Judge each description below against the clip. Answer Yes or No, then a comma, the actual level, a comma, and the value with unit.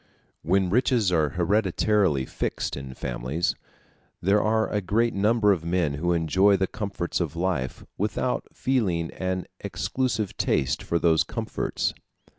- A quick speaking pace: No, slow, 135 wpm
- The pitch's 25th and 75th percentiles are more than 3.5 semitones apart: Yes, average, 4.0 semitones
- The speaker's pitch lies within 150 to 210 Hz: No, very low, 95 Hz